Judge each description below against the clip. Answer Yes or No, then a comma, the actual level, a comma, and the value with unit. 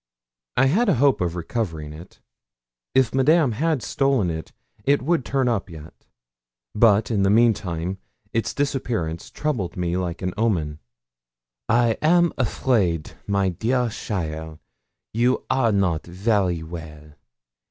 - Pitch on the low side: Yes, low, 105 Hz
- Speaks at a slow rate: Yes, slow, 130 wpm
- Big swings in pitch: Yes, wide, 7.1 semitones